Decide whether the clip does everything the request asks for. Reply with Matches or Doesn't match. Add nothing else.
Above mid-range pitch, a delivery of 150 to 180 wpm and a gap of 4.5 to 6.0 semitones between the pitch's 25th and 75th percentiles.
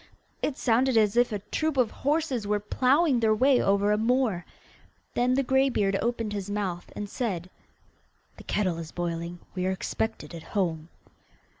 Matches